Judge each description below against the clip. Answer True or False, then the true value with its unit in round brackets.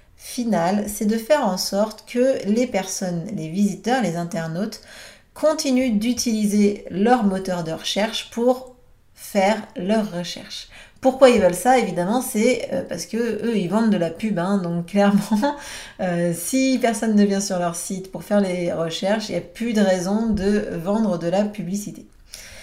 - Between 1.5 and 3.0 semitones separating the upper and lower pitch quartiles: False (3.8 semitones)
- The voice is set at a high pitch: True (205 Hz)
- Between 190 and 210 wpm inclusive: False (165 wpm)